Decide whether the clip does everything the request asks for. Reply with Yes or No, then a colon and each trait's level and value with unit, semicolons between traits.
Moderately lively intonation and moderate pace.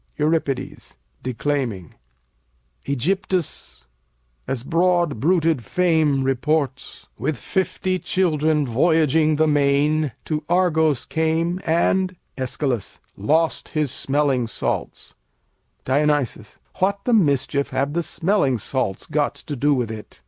No: average, 3.7 semitones; slow, 105 wpm